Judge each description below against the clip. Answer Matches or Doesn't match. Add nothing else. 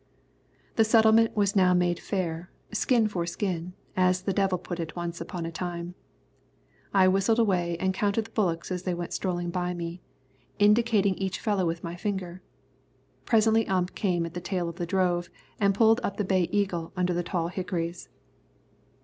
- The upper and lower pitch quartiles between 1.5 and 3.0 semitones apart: Matches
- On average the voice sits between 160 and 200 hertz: Matches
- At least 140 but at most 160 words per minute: Doesn't match